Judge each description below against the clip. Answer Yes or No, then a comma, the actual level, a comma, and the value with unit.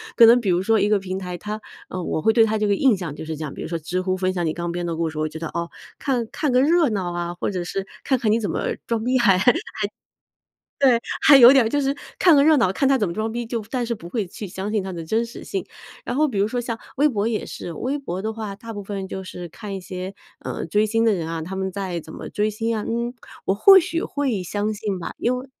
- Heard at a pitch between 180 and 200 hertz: No, high, 210 Hz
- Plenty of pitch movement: No, average, 4.6 semitones